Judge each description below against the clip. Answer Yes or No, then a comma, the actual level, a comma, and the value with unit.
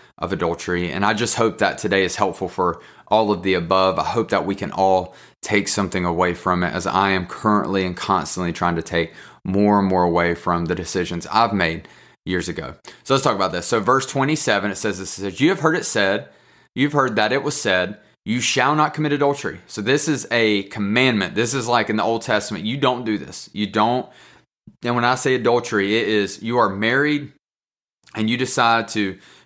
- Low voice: Yes, low, 105 Hz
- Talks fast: Yes, fast, 220 wpm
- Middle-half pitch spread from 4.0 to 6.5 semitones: Yes, average, 4.4 semitones